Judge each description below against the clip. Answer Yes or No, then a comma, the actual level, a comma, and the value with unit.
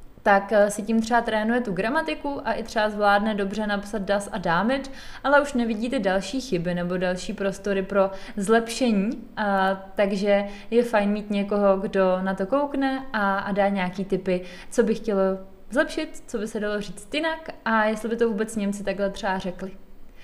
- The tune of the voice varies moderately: Yes, average, 3.1 semitones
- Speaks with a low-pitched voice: No, high, 210 Hz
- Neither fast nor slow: No, fast, 180 wpm